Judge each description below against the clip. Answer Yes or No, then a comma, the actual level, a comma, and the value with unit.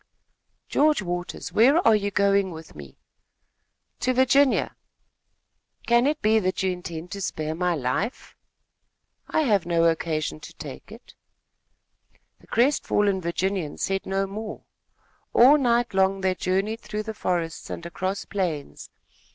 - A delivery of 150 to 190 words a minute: No, slow, 135 wpm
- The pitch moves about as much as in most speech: Yes, average, 4.5 semitones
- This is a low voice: No, high, 195 Hz